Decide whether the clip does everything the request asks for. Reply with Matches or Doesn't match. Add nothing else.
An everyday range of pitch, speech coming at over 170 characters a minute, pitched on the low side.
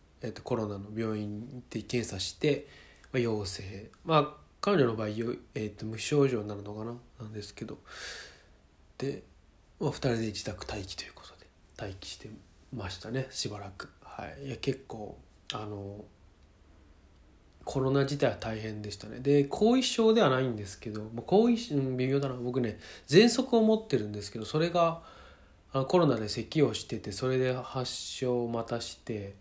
Matches